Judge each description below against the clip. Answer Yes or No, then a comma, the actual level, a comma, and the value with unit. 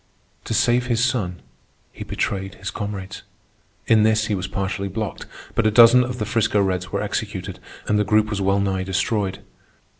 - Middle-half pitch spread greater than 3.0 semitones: No, narrow, 2.4 semitones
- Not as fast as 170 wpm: No, average, 180 wpm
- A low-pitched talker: Yes, low, 105 Hz